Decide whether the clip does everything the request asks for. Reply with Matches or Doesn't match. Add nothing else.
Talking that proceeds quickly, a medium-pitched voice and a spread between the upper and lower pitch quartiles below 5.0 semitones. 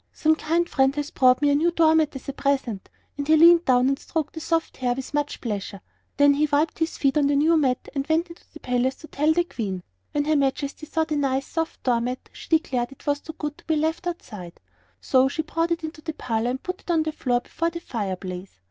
Doesn't match